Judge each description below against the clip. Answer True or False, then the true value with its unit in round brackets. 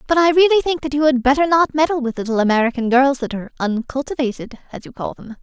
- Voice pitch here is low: False (270 Hz)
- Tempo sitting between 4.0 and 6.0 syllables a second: False (6.6 syllables/s)